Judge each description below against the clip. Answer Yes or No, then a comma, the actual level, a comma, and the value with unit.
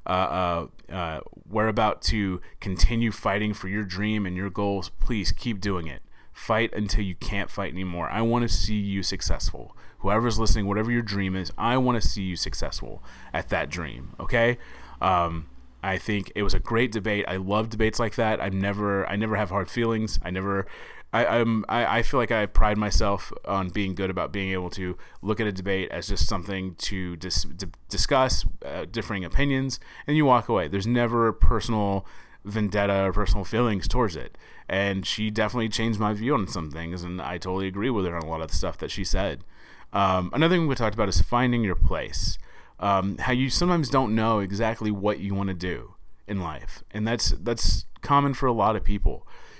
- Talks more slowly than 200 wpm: No, fast, 205 wpm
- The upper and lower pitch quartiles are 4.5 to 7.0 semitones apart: No, average, 3.1 semitones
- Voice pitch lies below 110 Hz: Yes, low, 100 Hz